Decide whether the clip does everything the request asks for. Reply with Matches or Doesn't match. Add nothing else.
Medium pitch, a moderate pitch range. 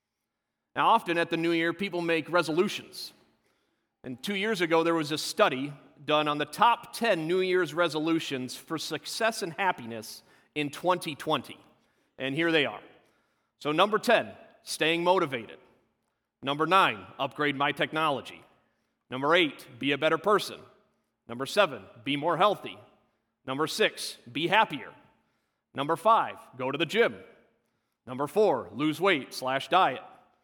Matches